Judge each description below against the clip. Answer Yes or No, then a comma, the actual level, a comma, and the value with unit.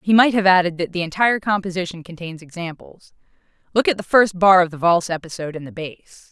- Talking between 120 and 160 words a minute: No, average, 200 wpm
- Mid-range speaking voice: Yes, medium, 180 Hz